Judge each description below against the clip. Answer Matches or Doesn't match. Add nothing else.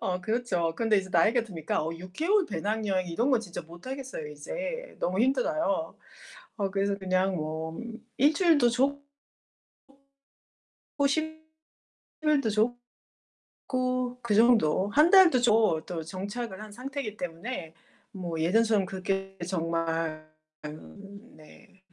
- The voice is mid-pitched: Doesn't match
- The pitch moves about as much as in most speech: Doesn't match